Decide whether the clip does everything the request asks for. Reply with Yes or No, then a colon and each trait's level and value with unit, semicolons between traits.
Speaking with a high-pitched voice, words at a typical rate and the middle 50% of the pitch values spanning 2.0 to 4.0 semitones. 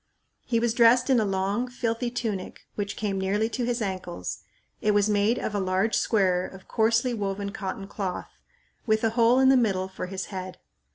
Yes: high, 210 Hz; average, 190 wpm; average, 3.3 semitones